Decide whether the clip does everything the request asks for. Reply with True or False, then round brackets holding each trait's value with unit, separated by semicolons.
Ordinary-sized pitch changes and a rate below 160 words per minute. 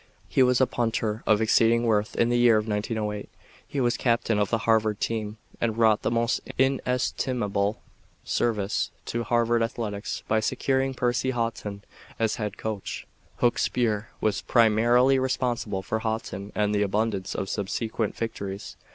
False (2.3 semitones; 150 wpm)